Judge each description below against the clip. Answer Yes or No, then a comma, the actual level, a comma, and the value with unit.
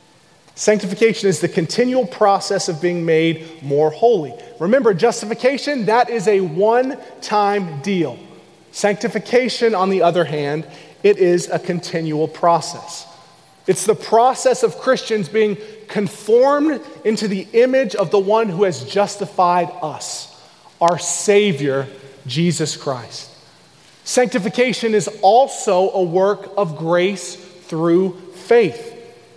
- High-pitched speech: Yes, high, 195 Hz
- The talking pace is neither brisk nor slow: No, slow, 115 wpm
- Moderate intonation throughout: Yes, average, 4.8 semitones